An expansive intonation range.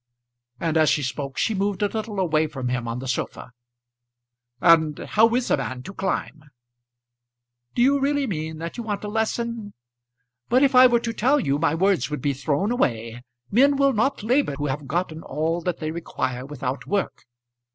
Yes: wide, 8.0 semitones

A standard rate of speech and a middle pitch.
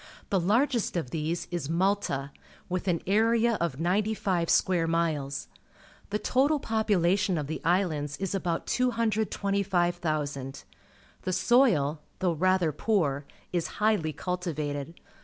No: slow, 125 wpm; medium, 180 Hz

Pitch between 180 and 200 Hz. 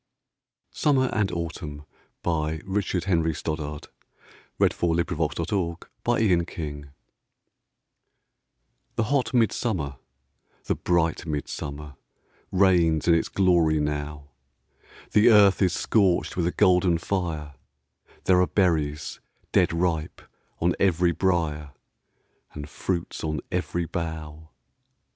No: very low, 85 Hz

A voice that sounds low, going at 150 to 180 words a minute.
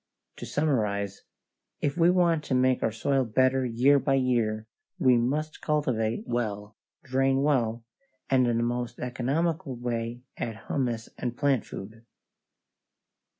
No: low, 125 Hz; slow, 135 wpm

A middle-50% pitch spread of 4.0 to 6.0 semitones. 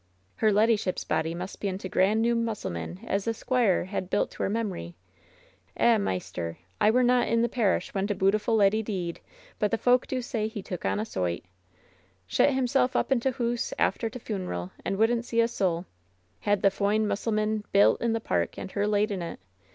No: average, 3.6 semitones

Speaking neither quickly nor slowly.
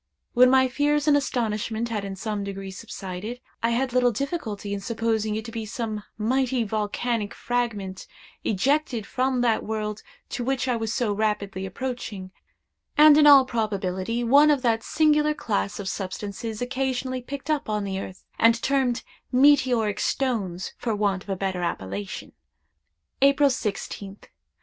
Yes: average, 155 wpm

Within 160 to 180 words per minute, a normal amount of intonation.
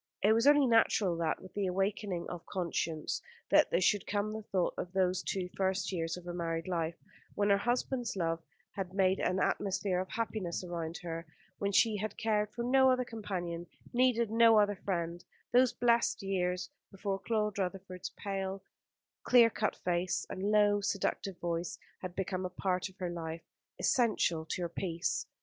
Yes: average, 170 wpm; average, 3.2 semitones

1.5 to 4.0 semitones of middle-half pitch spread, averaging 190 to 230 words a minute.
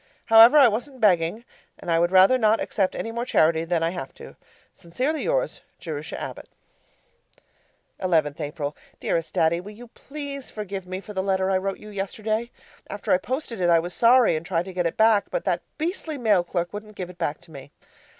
No: average, 5.2 semitones; average, 200 wpm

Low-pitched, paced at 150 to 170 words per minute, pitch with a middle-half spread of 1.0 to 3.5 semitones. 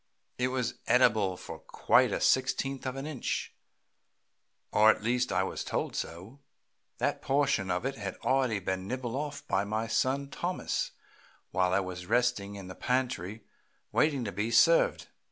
No: low, 120 Hz; average, 160 wpm; average, 5.0 semitones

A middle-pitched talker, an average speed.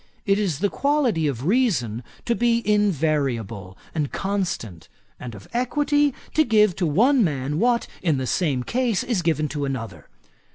Yes: medium, 175 Hz; average, 160 wpm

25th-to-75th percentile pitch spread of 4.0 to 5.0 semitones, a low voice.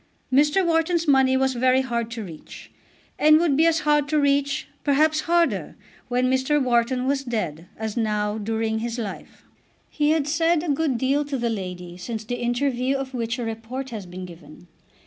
No: average, 4.7 semitones; very high, 260 Hz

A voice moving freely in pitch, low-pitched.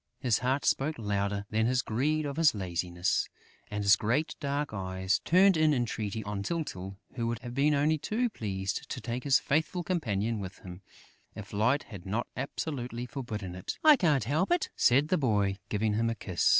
Yes: wide, 6.4 semitones; low, 115 Hz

